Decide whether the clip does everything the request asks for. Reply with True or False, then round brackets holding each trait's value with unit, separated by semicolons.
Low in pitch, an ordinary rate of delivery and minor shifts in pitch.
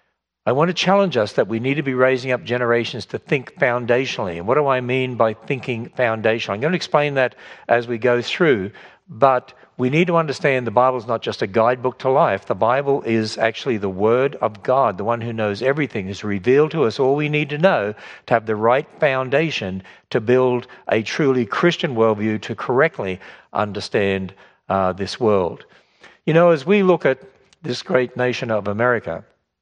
False (125 Hz; 195 wpm; 3.7 semitones)